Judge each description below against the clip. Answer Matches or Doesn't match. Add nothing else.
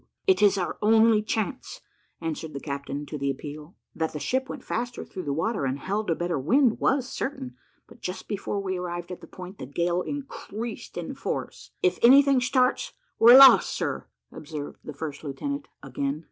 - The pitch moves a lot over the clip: Matches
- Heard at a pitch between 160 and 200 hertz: Matches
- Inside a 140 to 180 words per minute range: Doesn't match